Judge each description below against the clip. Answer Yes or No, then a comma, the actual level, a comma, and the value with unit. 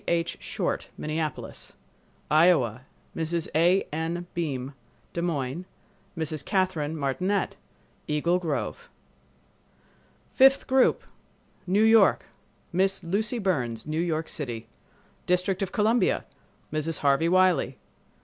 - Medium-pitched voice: Yes, medium, 165 Hz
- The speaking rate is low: Yes, slow, 90 wpm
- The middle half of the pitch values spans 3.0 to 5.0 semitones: Yes, average, 3.8 semitones